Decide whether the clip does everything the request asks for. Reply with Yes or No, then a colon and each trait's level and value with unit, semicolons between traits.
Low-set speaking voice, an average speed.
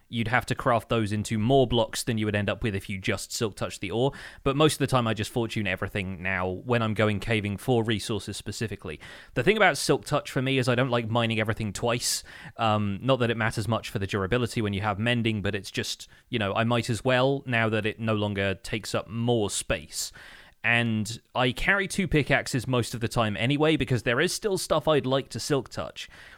No: low, 115 Hz; fast, 235 wpm